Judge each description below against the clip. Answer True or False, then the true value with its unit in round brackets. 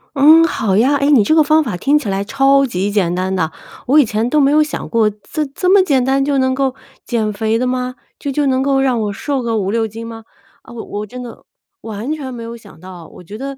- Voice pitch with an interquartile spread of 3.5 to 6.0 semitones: True (4.7 semitones)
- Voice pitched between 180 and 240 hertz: False (250 Hz)